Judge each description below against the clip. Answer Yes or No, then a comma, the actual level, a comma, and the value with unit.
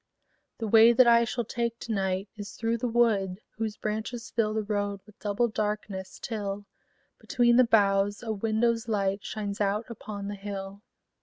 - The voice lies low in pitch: No, high, 215 Hz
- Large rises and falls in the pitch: No, narrow, 2.4 semitones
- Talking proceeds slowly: No, average, 170 wpm